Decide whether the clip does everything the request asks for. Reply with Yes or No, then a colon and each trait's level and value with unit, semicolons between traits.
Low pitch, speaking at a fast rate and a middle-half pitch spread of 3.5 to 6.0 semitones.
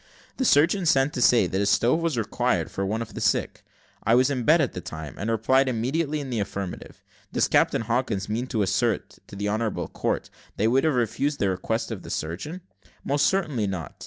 Yes: low, 115 Hz; fast, 220 wpm; wide, 5.6 semitones